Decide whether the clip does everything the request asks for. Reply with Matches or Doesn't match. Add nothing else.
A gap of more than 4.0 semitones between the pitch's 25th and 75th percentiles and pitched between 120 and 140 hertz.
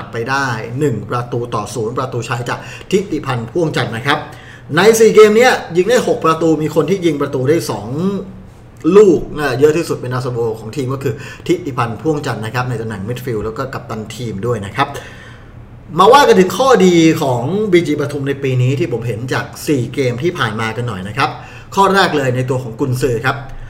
Matches